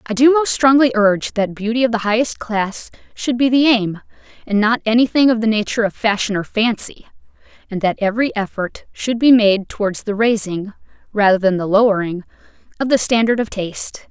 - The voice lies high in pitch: Yes, high, 220 Hz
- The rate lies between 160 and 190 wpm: Yes, average, 185 wpm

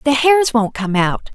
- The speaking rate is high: Yes, fast, 220 wpm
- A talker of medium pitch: No, very high, 250 Hz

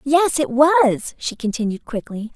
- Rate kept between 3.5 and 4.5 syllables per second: Yes, 4.1 syllables/s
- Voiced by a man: No, female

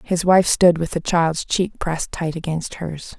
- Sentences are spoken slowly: No, fast, 205 wpm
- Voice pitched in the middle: Yes, medium, 170 Hz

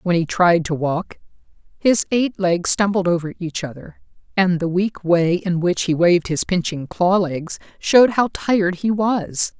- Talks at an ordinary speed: Yes, average, 180 wpm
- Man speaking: No, female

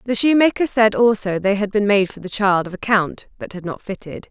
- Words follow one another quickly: Yes, fast, 250 wpm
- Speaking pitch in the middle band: No, high, 205 Hz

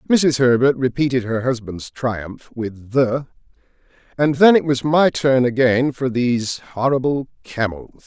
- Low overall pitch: Yes, low, 130 Hz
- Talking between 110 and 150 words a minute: Yes, average, 140 wpm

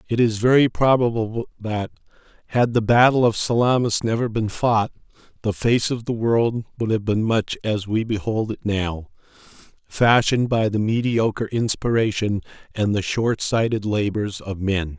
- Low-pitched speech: Yes, low, 110 Hz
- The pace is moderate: Yes, average, 155 wpm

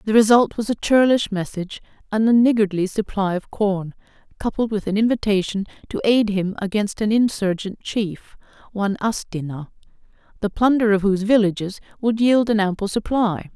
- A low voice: No, high, 210 Hz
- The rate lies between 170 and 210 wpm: No, average, 155 wpm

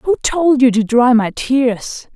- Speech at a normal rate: Yes, average, 195 wpm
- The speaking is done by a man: No, female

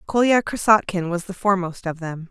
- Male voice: No, female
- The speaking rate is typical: Yes, average, 180 wpm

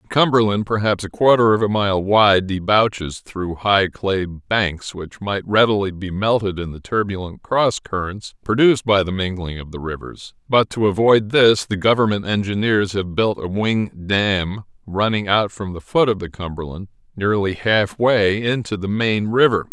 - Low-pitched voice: Yes, low, 100 Hz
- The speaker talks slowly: No, average, 175 wpm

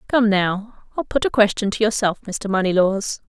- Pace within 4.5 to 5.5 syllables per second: Yes, 5.0 syllables/s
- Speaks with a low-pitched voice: No, high, 210 Hz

